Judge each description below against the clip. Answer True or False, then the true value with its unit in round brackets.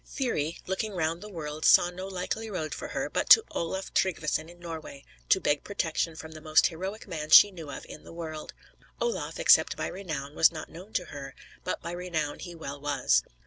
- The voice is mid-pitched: True (165 Hz)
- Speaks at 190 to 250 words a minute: True (205 wpm)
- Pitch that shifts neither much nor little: True (3.2 semitones)